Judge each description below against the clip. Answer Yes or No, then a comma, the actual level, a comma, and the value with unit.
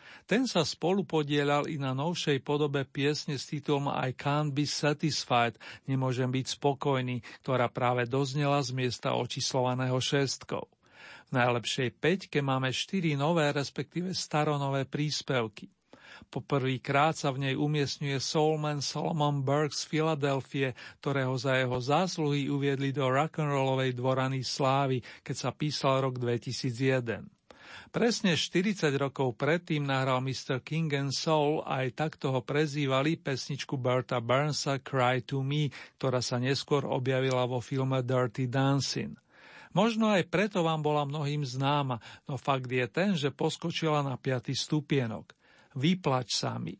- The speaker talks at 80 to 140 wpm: Yes, average, 135 wpm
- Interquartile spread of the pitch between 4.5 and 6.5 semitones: No, narrow, 2.5 semitones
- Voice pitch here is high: No, medium, 140 Hz